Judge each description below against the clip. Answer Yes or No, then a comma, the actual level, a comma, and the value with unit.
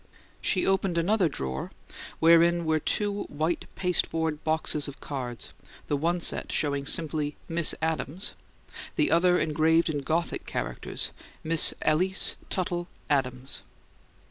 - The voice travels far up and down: No, average, 2.9 semitones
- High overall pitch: No, medium, 160 Hz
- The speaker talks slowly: Yes, slow, 120 wpm